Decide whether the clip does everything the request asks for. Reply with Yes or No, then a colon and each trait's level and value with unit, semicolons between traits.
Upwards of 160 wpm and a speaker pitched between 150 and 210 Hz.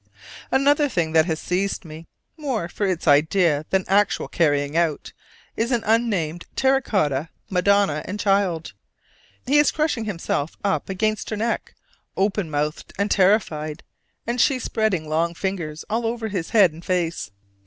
No: average, 155 wpm; high, 190 Hz